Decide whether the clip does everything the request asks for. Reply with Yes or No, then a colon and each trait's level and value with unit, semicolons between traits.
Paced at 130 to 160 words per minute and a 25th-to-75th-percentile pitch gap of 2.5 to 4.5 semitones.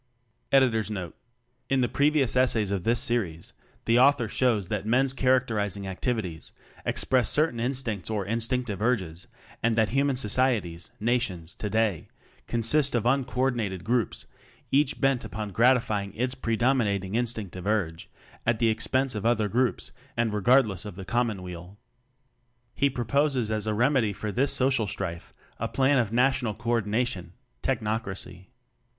Yes: average, 145 wpm; average, 3.8 semitones